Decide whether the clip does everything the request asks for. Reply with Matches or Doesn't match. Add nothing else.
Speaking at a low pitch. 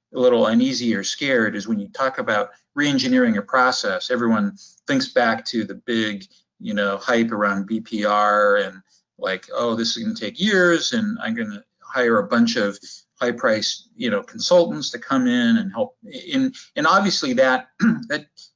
Doesn't match